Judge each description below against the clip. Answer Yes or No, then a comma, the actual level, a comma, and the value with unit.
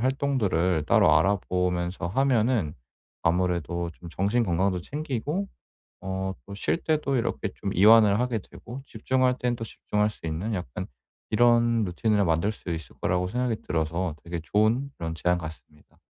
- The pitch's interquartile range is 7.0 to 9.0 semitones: No, average, 5.3 semitones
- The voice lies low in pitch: Yes, low, 100 Hz